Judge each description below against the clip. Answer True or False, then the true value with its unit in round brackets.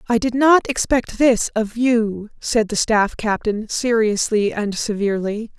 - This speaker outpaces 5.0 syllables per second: False (4.1 syllables/s)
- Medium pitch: False (220 Hz)